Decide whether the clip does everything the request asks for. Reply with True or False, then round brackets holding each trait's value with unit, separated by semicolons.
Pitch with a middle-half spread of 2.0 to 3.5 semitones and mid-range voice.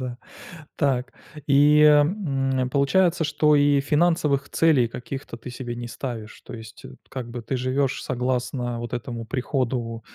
False (3.0 semitones; 130 Hz)